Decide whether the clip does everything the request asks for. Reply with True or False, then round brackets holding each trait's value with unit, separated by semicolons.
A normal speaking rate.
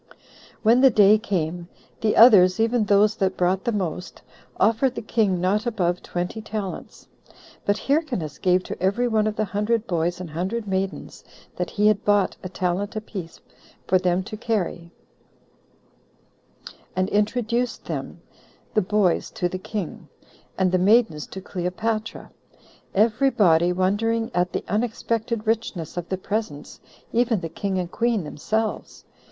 True (145 wpm)